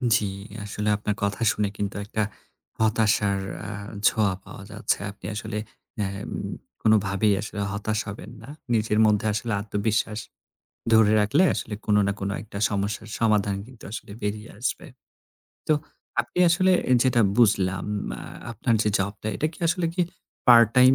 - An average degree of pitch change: No, narrow, 1.8 semitones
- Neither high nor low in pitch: No, low, 105 Hz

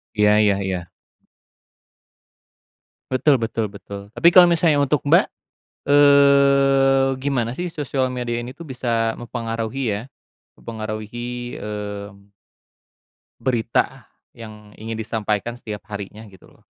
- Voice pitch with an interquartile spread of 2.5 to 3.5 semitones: No, average, 4.1 semitones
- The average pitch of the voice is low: Yes, low, 120 Hz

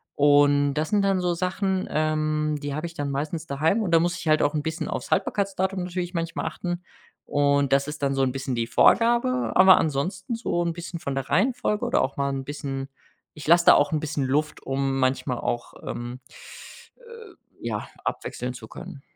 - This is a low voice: No, medium, 155 Hz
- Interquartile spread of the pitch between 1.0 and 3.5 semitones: No, average, 4.6 semitones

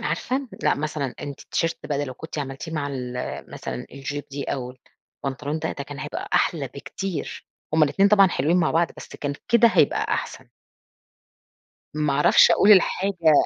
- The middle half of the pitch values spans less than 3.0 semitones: No, average, 3.6 semitones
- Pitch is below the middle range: No, medium, 150 Hz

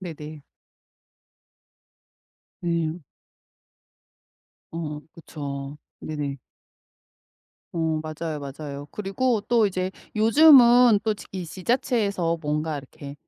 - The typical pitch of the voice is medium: Yes, medium, 165 Hz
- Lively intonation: Yes, wide, 5.8 semitones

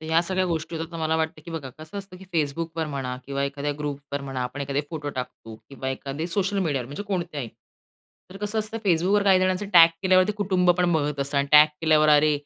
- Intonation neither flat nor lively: Yes, average, 4.4 semitones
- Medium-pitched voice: Yes, medium, 160 Hz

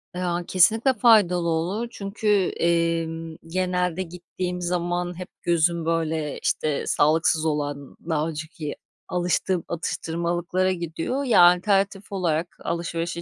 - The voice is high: No, medium, 175 Hz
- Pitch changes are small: Yes, narrow, 2.0 semitones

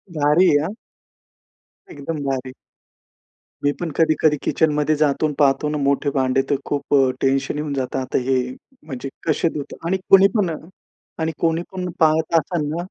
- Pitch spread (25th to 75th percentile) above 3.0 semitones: No, average, 2.7 semitones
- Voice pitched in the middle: Yes, medium, 150 Hz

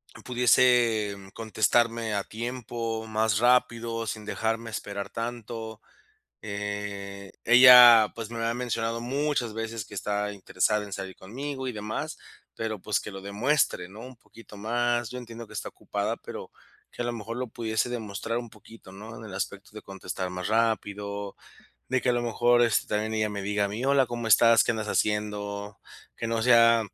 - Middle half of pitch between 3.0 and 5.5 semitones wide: No, narrow, 2.5 semitones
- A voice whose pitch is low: Yes, low, 110 Hz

